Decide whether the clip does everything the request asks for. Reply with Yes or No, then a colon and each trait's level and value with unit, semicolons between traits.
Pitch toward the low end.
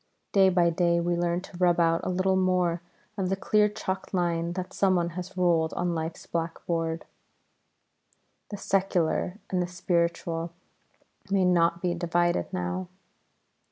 No: medium, 175 Hz